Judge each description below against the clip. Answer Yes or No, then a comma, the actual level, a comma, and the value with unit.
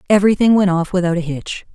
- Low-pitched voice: No, medium, 185 Hz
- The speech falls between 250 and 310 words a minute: No, fast, 205 wpm